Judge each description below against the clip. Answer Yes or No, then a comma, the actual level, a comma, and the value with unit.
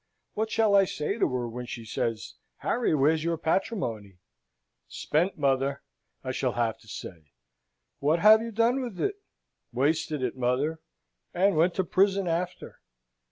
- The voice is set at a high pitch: No, medium, 155 Hz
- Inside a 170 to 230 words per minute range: No, average, 155 wpm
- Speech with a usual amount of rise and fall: No, wide, 7.5 semitones